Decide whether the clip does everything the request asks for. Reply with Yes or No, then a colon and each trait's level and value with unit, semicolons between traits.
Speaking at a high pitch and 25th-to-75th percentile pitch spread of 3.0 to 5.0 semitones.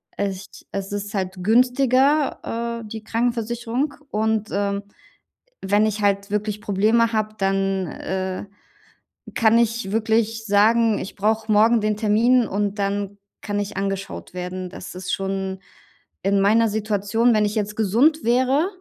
No: high, 210 Hz; narrow, 2.5 semitones